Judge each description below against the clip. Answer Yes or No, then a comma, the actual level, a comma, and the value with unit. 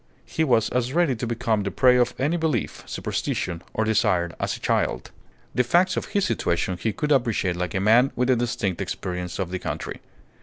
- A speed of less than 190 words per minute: No, average, 200 wpm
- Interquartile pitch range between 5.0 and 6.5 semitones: Yes, wide, 5.5 semitones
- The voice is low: Yes, low, 115 Hz